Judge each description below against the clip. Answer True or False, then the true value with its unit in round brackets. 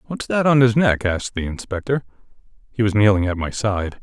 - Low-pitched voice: True (110 Hz)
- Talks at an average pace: True (195 wpm)